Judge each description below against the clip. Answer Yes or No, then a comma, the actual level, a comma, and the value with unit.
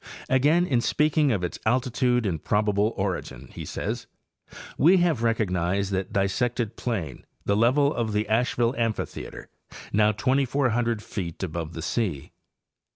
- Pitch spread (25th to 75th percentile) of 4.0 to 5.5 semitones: Yes, average, 4.5 semitones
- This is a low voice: Yes, low, 110 Hz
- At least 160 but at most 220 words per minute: No, average, 140 wpm